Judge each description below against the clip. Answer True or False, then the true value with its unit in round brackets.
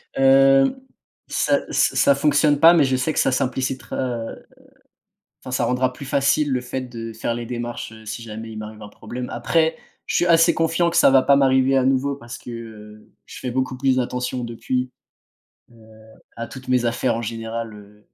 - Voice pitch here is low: True (125 Hz)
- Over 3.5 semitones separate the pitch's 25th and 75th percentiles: False (2.8 semitones)